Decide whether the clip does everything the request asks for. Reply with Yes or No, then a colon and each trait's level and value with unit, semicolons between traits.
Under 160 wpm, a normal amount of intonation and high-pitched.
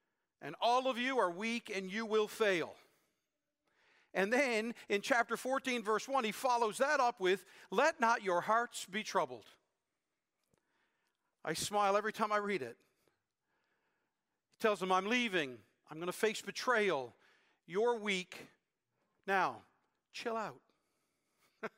Yes: average, 140 wpm; average, 3.4 semitones; high, 220 Hz